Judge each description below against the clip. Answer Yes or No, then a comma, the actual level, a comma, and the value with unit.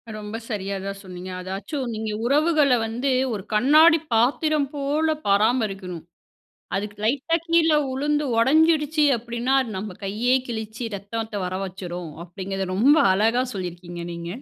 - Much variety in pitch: Yes, wide, 6.3 semitones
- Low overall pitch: No, high, 225 Hz